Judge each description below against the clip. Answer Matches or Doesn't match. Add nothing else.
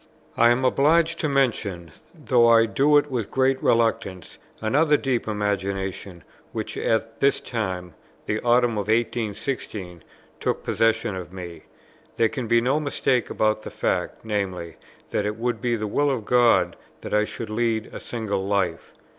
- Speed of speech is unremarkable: Matches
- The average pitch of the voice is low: Matches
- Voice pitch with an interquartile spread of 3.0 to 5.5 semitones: Matches